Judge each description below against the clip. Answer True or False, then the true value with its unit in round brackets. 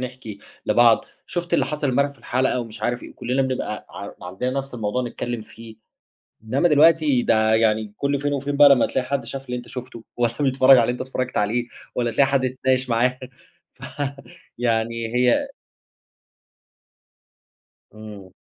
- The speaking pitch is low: True (125 Hz)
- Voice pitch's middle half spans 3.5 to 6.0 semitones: False (2.8 semitones)